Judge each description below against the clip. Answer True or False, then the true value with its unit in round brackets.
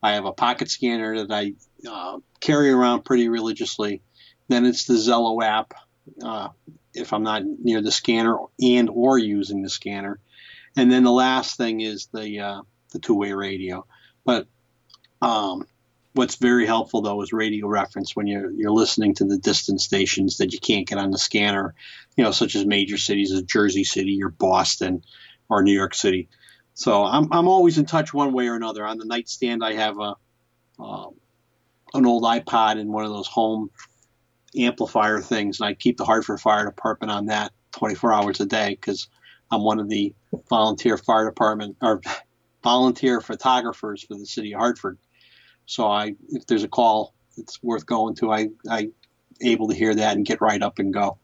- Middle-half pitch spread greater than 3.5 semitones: False (2.7 semitones)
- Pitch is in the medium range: False (110 Hz)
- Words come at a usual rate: True (185 wpm)